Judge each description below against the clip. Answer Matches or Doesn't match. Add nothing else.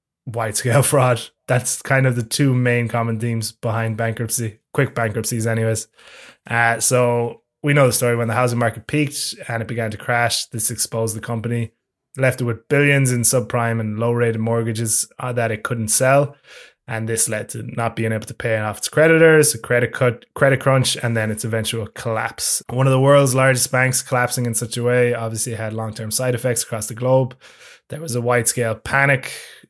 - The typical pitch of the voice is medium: Doesn't match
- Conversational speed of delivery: Matches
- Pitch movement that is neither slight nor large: Doesn't match